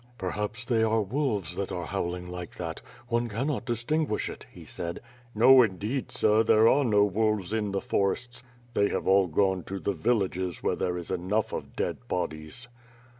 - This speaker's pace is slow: No, average, 175 wpm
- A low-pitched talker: Yes, low, 105 Hz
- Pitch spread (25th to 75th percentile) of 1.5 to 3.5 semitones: No, average, 3.9 semitones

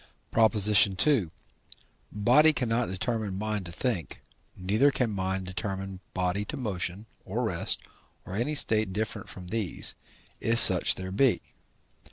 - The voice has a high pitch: No, low, 105 Hz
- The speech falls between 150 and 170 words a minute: No, slow, 135 wpm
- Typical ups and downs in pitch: Yes, average, 3.4 semitones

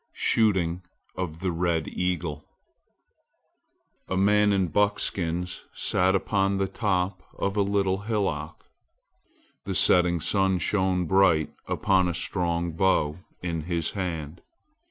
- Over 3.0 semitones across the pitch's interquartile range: No, narrow, 2.4 semitones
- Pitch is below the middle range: Yes, very low, 90 Hz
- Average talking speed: No, slow, 115 wpm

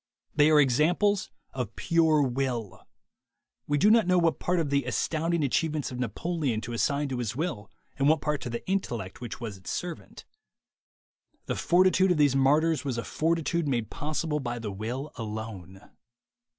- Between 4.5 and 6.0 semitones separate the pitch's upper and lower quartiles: Yes, wide, 5.5 semitones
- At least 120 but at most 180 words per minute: Yes, average, 175 wpm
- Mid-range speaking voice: Yes, medium, 145 Hz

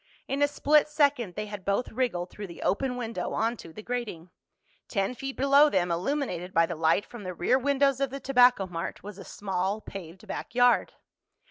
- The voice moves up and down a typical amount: No, wide, 6.5 semitones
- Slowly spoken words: No, average, 195 wpm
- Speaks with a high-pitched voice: Yes, high, 220 Hz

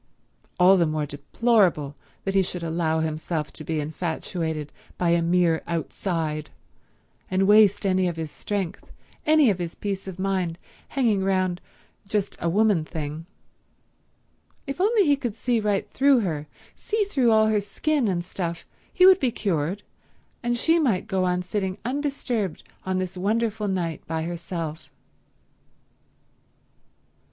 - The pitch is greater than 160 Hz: Yes, medium, 185 Hz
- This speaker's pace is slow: No, average, 145 wpm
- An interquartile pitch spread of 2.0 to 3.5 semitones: No, average, 4.7 semitones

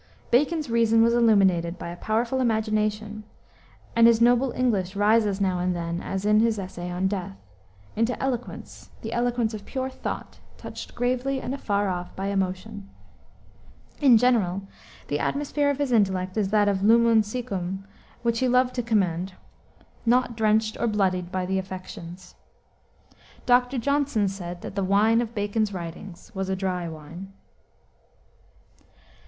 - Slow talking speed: No, average, 150 wpm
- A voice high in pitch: Yes, high, 210 Hz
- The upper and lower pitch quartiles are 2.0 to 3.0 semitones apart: No, average, 3.9 semitones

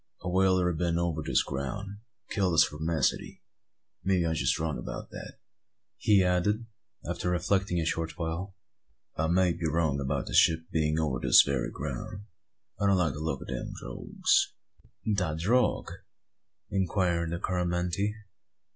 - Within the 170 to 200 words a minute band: No, average, 155 wpm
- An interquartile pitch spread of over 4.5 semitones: No, average, 2.9 semitones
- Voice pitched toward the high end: No, very low, 85 Hz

